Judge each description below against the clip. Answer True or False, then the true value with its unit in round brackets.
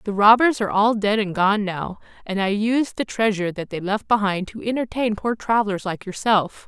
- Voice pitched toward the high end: True (210 Hz)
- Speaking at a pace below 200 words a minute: False (205 wpm)